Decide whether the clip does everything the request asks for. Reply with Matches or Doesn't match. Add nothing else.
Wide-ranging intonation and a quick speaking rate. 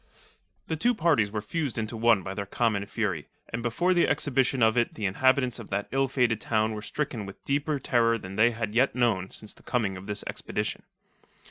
Doesn't match